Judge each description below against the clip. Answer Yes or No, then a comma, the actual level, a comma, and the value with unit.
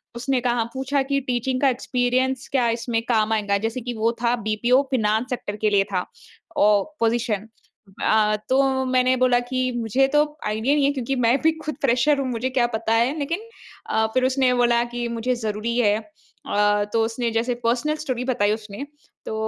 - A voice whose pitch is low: No, high, 240 Hz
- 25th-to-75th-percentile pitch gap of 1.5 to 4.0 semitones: Yes, average, 2.8 semitones